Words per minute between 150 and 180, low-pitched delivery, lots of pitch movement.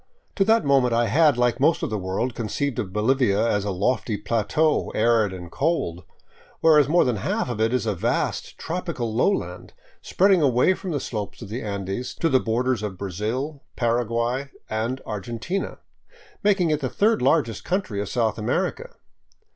Yes: average, 170 wpm; low, 120 Hz; wide, 5.9 semitones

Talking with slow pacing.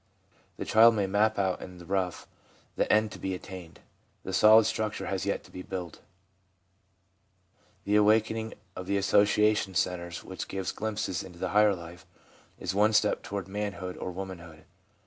No: average, 165 wpm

